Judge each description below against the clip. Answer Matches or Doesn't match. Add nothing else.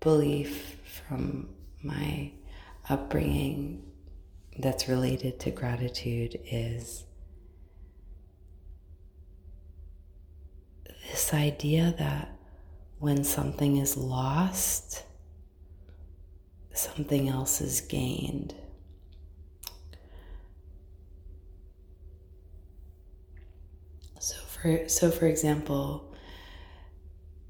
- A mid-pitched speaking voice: Doesn't match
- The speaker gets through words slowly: Matches